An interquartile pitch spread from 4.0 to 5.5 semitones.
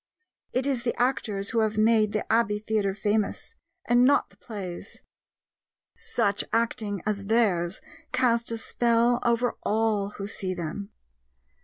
No: average, 2.7 semitones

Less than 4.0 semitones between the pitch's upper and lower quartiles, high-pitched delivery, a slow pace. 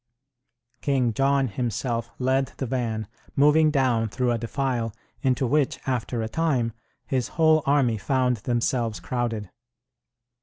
No: average, 2.8 semitones; low, 125 Hz; slow, 125 wpm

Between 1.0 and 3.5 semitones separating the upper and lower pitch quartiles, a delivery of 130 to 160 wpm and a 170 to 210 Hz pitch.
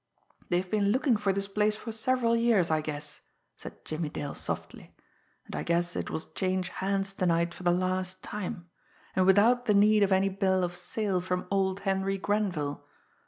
No: average, 2.7 semitones; average, 185 wpm; high, 190 Hz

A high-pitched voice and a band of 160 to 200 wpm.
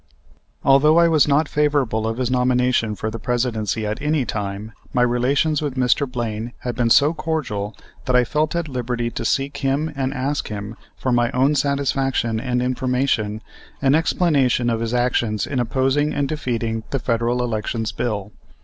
No: low, 125 Hz; average, 170 wpm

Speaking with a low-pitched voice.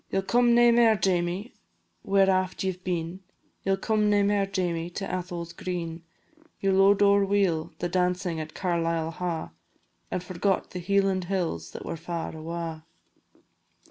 No: medium, 185 Hz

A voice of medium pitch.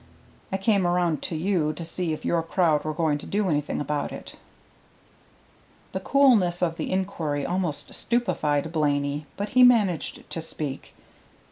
Yes: medium, 170 Hz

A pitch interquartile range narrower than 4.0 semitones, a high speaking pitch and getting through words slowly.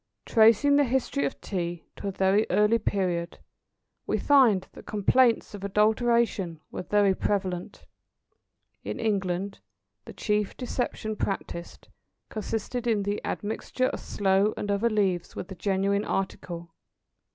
Yes: average, 2.7 semitones; high, 205 Hz; slow, 130 wpm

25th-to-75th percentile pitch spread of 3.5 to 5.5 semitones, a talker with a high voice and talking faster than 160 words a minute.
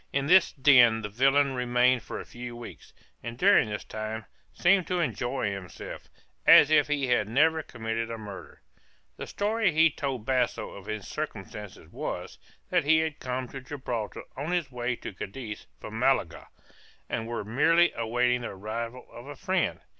No: average, 4.6 semitones; low, 125 Hz; average, 170 wpm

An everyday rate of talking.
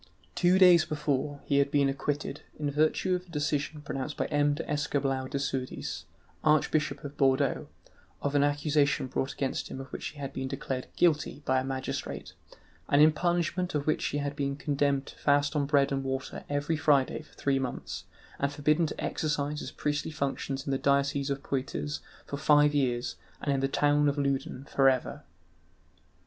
Yes: average, 185 wpm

